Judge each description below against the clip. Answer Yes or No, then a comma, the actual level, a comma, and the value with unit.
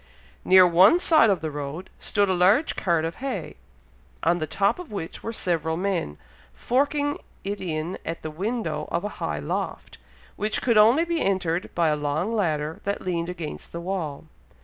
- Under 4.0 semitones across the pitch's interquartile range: No, average, 4.6 semitones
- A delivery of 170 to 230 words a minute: Yes, average, 180 wpm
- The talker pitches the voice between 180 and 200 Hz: Yes, medium, 185 Hz